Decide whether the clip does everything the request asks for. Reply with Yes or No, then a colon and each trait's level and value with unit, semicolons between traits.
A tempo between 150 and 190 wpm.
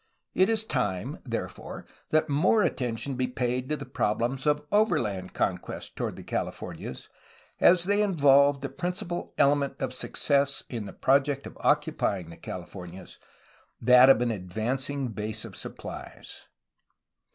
No: average, 140 wpm